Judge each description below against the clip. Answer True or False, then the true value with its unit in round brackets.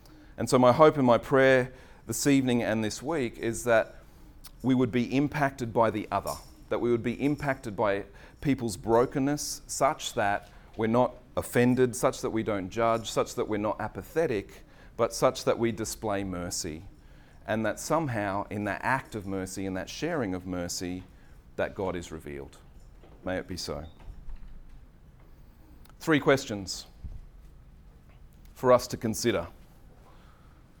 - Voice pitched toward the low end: True (110 Hz)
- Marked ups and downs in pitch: True (5.9 semitones)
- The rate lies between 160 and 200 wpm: False (150 wpm)